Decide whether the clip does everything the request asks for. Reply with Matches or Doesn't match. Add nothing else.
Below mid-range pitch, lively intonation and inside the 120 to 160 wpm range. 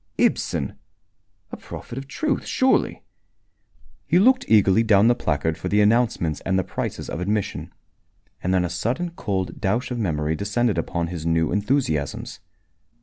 Matches